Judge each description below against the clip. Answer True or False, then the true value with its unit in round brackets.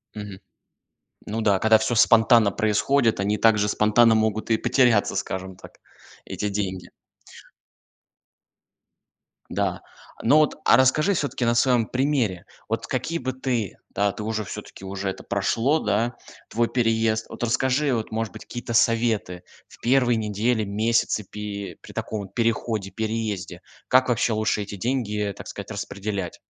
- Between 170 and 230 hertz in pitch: False (110 Hz)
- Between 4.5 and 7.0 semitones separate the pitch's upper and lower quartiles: False (2.7 semitones)